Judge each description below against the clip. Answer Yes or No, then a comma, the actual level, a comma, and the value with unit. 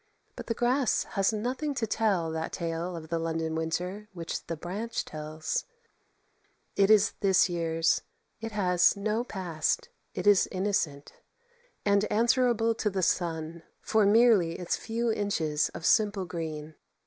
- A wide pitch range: No, average, 4.8 semitones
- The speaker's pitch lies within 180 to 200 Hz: Yes, high, 190 Hz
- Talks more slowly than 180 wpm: Yes, average, 145 wpm